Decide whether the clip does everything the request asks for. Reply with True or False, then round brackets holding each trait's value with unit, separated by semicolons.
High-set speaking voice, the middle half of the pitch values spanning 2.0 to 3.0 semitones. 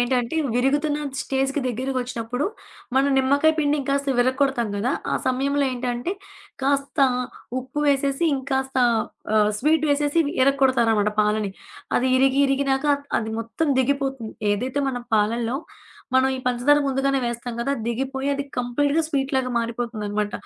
True (265 Hz; 2.5 semitones)